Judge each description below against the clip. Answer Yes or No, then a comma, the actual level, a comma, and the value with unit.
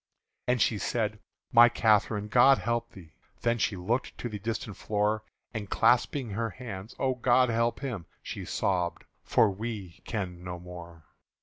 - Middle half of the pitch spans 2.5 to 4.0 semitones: Yes, average, 3.6 semitones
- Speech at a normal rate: Yes, average, 160 wpm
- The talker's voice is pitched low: Yes, low, 110 Hz